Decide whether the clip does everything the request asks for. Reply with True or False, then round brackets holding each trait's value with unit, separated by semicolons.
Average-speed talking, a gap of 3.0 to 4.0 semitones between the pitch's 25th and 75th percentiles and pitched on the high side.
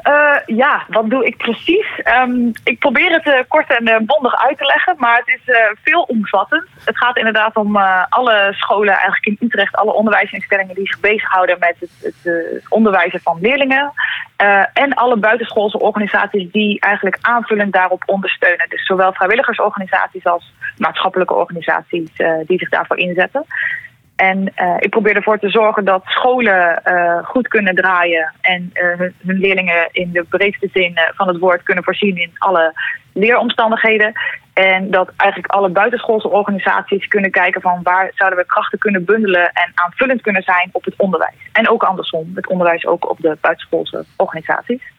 True (170 wpm; 3.6 semitones; 200 Hz)